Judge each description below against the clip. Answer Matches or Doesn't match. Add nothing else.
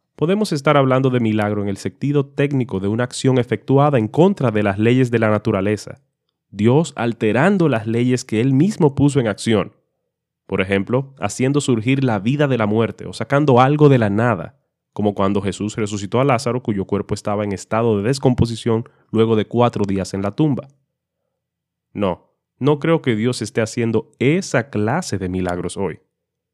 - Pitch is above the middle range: Doesn't match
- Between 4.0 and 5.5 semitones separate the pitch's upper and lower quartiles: Matches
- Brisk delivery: Doesn't match